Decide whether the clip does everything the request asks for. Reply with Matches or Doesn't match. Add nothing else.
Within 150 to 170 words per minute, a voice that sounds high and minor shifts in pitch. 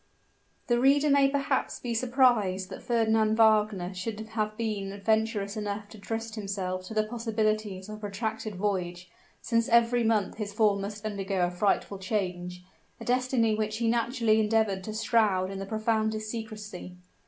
Matches